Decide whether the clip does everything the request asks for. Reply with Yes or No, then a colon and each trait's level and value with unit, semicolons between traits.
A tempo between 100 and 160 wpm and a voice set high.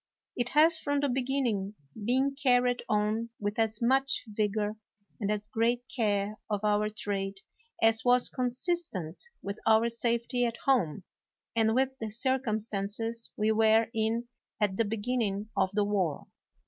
Yes: average, 150 wpm; high, 225 Hz